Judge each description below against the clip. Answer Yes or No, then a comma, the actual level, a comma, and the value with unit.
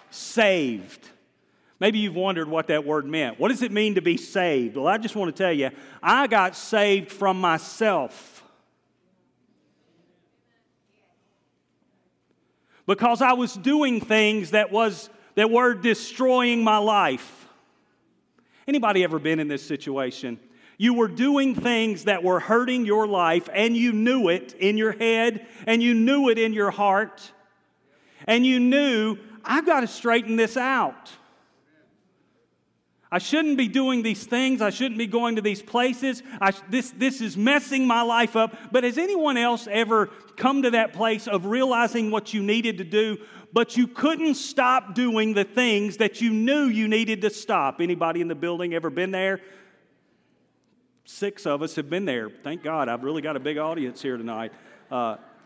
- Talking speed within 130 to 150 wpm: No, average, 165 wpm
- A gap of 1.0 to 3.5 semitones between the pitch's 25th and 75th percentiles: No, average, 3.9 semitones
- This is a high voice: Yes, high, 220 Hz